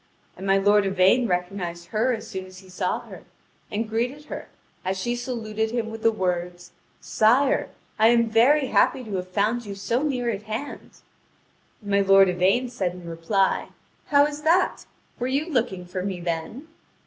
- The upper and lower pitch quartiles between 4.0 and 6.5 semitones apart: Yes, average, 4.6 semitones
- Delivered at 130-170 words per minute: No, average, 180 wpm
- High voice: Yes, high, 215 Hz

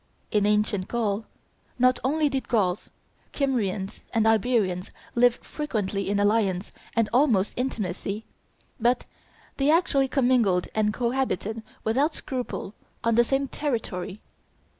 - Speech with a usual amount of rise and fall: Yes, average, 4.1 semitones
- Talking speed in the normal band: No, slow, 120 wpm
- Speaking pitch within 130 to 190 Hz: No, high, 225 Hz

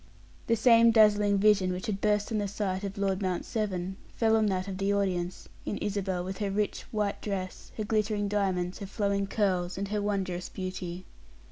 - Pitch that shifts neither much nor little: No, narrow, 2.0 semitones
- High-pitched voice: Yes, high, 200 Hz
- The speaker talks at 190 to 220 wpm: Yes, average, 195 wpm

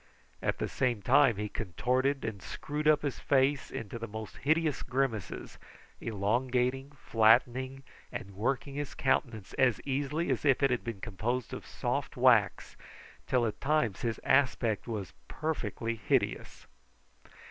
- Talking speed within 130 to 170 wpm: Yes, average, 140 wpm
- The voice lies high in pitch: No, low, 125 Hz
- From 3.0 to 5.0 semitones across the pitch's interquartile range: Yes, average, 3.8 semitones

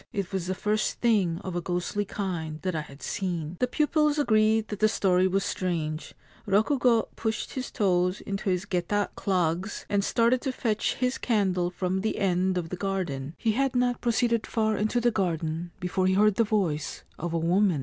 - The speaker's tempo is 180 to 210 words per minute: Yes, average, 200 wpm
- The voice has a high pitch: Yes, high, 195 Hz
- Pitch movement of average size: Yes, average, 3.6 semitones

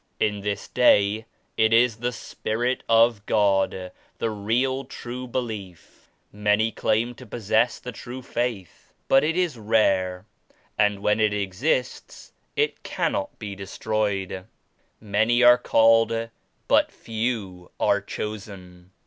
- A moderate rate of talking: No, slow, 125 wpm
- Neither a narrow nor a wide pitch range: Yes, average, 3.1 semitones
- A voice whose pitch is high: No, low, 110 Hz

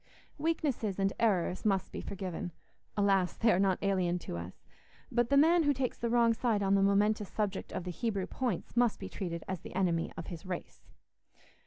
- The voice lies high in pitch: Yes, high, 195 Hz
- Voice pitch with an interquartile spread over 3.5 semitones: Yes, average, 4.2 semitones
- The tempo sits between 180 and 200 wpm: Yes, average, 185 wpm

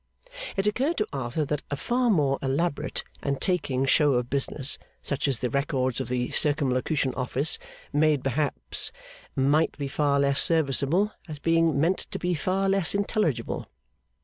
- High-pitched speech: No, medium, 145 Hz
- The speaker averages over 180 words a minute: No, average, 155 wpm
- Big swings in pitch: No, average, 3.5 semitones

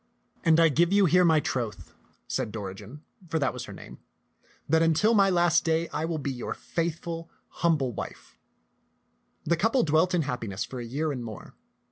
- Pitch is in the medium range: Yes, medium, 160 Hz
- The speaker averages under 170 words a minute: No, average, 190 wpm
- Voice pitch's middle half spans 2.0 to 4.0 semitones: No, average, 4.6 semitones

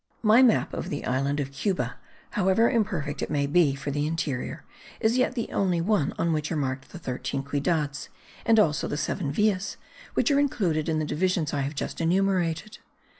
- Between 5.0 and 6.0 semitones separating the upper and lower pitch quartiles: Yes, wide, 5.5 semitones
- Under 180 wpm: No, average, 185 wpm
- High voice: No, medium, 165 Hz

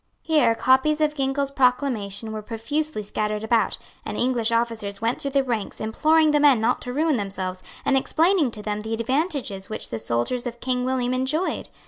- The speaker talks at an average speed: Yes, average, 180 wpm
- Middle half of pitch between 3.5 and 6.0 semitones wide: Yes, average, 4.5 semitones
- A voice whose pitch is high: Yes, very high, 250 Hz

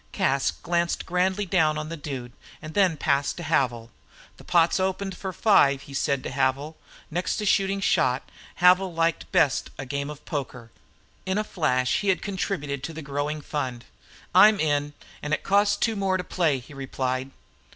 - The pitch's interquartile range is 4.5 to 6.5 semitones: Yes, average, 5.3 semitones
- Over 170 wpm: Yes, average, 180 wpm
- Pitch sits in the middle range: Yes, medium, 155 Hz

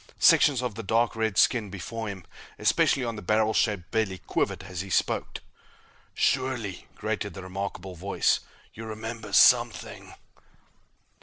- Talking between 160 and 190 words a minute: No, average, 140 wpm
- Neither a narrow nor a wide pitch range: Yes, average, 3.0 semitones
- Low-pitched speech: Yes, low, 110 Hz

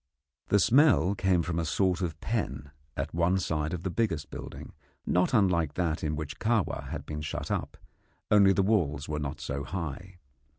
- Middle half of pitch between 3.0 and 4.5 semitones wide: Yes, average, 4.2 semitones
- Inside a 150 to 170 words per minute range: No, average, 180 wpm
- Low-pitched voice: Yes, very low, 85 Hz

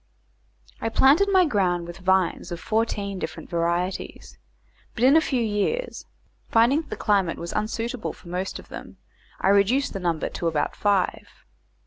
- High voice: Yes, high, 200 Hz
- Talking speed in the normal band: Yes, average, 160 wpm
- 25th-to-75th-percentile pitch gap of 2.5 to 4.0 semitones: No, average, 5.1 semitones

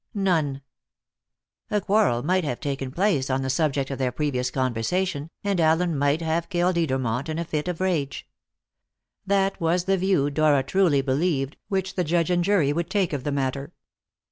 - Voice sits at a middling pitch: Yes, medium, 155 Hz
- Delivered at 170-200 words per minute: Yes, average, 175 wpm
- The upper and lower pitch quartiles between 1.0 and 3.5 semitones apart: No, average, 4.7 semitones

